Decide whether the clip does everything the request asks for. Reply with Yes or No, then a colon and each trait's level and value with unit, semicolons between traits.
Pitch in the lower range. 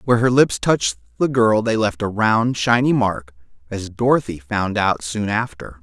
Yes: low, 110 Hz